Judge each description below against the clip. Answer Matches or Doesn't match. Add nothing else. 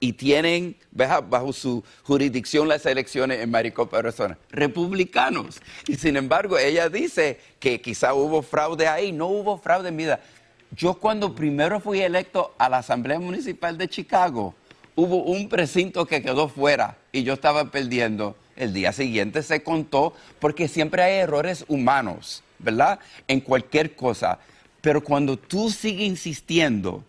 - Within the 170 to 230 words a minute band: Doesn't match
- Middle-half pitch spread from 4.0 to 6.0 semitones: Matches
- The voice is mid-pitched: Matches